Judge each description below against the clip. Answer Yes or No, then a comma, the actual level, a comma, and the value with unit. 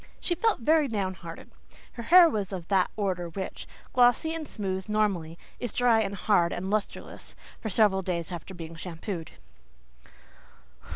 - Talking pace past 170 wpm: No, average, 155 wpm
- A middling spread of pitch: Yes, average, 4.6 semitones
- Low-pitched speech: No, high, 195 Hz